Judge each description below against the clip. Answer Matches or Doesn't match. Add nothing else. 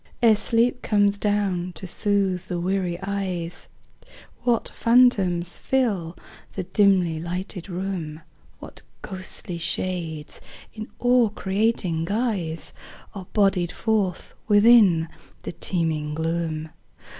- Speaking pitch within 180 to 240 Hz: Matches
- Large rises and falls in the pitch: Doesn't match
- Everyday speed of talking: Doesn't match